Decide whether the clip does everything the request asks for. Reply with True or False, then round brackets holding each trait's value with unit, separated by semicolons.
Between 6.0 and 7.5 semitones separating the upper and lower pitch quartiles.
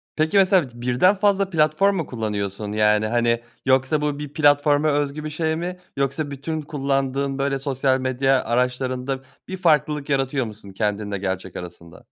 False (4.1 semitones)